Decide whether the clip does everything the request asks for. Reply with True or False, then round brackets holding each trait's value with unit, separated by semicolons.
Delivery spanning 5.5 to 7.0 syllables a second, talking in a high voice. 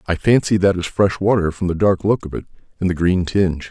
False (5.9 syllables/s; 95 Hz)